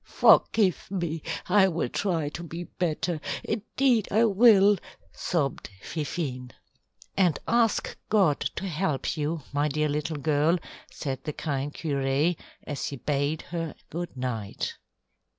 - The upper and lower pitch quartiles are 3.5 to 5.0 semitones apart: Yes, average, 4.6 semitones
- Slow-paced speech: Yes, slow, 130 wpm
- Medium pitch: Yes, medium, 160 Hz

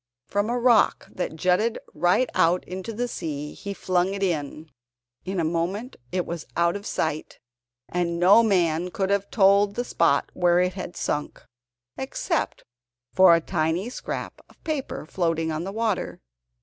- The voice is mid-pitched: Yes, medium, 180 Hz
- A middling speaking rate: Yes, average, 160 wpm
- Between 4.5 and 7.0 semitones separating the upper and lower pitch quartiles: No, average, 3.3 semitones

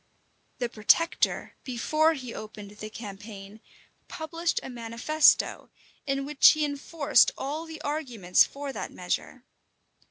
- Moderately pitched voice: No, very high, 275 Hz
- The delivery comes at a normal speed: No, slow, 120 wpm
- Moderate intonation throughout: No, wide, 6.0 semitones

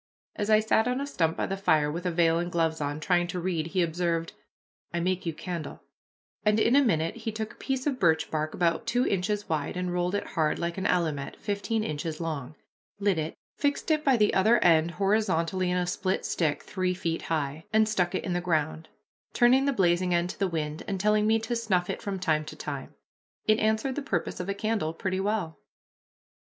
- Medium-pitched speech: Yes, medium, 180 Hz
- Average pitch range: Yes, average, 4.5 semitones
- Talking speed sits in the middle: No, fast, 220 wpm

